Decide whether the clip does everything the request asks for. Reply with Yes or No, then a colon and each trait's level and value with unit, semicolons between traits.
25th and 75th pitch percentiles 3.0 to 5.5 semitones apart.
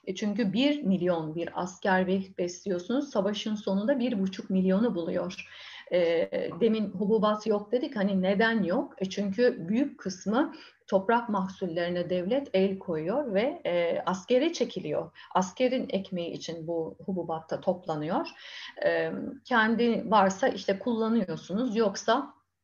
Yes: average, 4.7 semitones